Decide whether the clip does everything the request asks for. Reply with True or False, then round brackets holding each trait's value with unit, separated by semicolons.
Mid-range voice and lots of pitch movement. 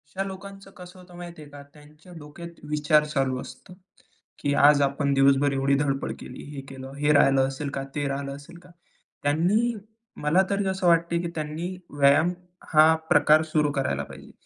False (150 Hz; 3.8 semitones)